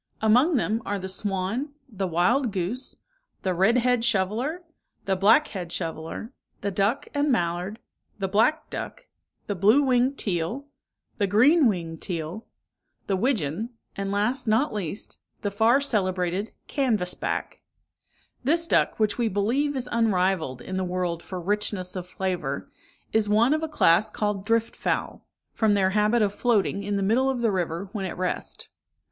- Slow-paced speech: No, average, 160 wpm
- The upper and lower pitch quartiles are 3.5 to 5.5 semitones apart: Yes, average, 4.4 semitones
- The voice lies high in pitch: Yes, high, 205 Hz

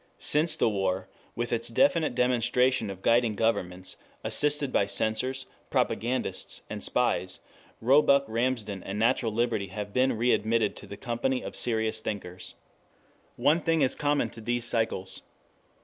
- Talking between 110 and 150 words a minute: Yes, average, 140 wpm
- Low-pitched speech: Yes, low, 115 Hz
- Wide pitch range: No, average, 3.6 semitones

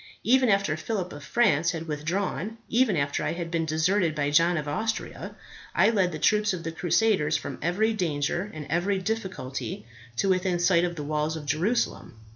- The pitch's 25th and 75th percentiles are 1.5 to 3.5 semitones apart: No, average, 4.7 semitones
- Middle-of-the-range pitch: Yes, medium, 175 Hz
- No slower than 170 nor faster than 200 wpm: Yes, average, 185 wpm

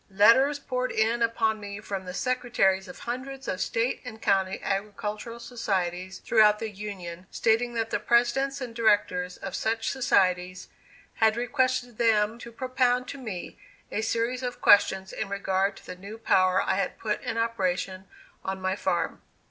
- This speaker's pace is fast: No, average, 165 wpm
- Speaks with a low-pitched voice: No, high, 220 Hz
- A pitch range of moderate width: Yes, average, 3.9 semitones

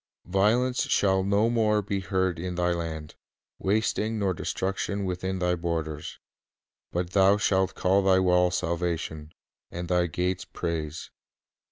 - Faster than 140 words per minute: No, slow, 135 wpm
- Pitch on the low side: Yes, very low, 90 Hz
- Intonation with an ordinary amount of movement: No, narrow, 2.2 semitones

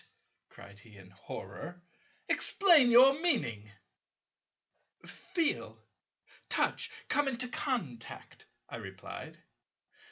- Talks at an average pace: No, slow, 85 wpm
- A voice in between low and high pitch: No, high, 235 Hz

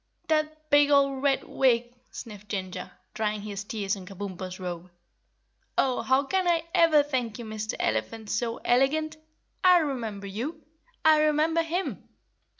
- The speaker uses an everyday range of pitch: No, wide, 6.8 semitones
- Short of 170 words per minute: Yes, average, 145 wpm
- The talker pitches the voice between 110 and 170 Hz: No, very high, 250 Hz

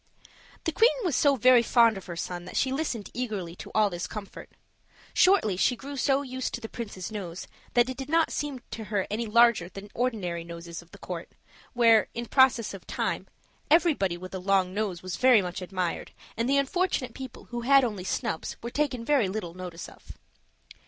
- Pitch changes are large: Yes, wide, 5.8 semitones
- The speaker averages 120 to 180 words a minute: No, average, 200 wpm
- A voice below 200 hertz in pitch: No, high, 225 Hz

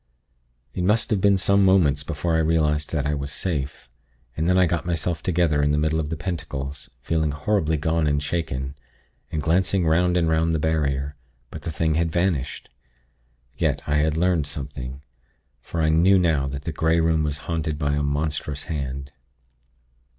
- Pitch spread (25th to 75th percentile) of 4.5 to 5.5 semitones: No, narrow, 2.6 semitones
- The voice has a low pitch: Yes, very low, 80 Hz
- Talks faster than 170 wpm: Yes, average, 180 wpm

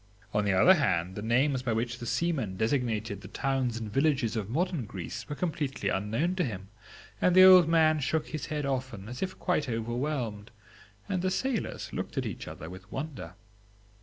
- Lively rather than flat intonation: Yes, wide, 6.1 semitones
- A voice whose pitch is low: Yes, low, 130 Hz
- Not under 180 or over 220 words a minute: Yes, average, 190 wpm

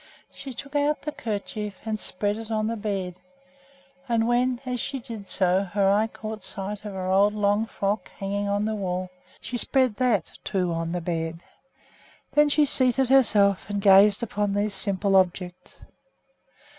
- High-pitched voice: Yes, high, 205 Hz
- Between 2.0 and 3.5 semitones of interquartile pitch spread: Yes, average, 3.0 semitones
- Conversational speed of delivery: Yes, average, 170 wpm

